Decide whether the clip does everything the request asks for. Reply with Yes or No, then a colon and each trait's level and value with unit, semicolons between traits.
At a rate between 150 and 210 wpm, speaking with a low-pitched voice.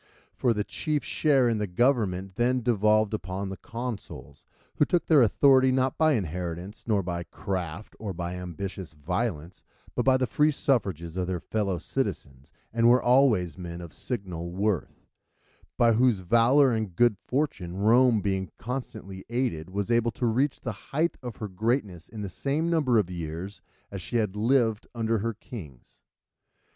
Yes: average, 170 wpm; low, 110 Hz